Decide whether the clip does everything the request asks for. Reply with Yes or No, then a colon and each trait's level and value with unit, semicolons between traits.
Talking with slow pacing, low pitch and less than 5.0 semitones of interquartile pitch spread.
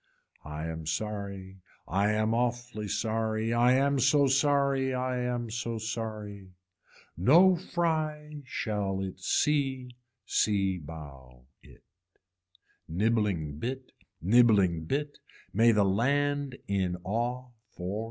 No: slow, 110 wpm; low, 115 Hz; average, 5.3 semitones